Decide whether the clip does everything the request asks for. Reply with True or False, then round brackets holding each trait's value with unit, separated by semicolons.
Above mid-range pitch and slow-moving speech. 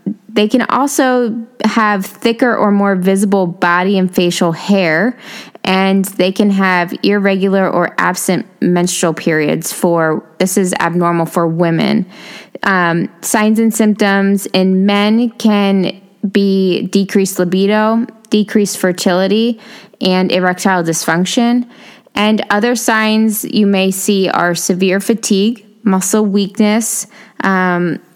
True (200 Hz; 115 wpm)